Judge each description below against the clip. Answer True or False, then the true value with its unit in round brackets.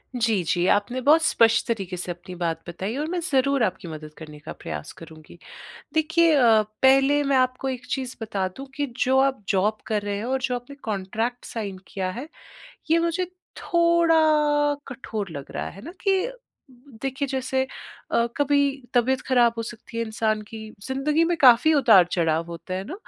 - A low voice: False (235 Hz)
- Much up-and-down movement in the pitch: True (5.9 semitones)